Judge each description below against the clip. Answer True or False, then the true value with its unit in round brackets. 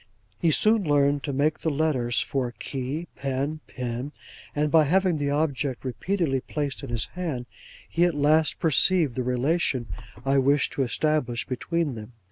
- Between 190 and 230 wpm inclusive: False (160 wpm)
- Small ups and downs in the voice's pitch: False (3.5 semitones)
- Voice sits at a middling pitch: True (145 Hz)